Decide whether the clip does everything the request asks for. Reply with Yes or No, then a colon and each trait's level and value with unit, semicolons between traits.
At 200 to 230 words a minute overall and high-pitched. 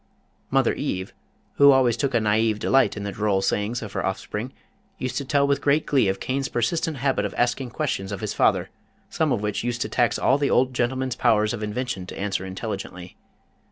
No: fast, 205 wpm; low, 120 Hz